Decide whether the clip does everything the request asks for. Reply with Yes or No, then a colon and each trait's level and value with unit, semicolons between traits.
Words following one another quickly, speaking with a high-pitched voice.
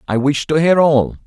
No: fast, 240 wpm; medium, 140 Hz